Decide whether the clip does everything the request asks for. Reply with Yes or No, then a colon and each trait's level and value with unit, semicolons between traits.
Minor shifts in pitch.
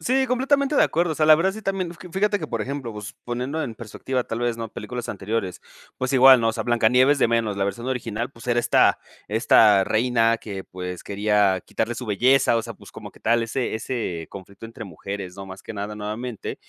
No: average, 4.0 semitones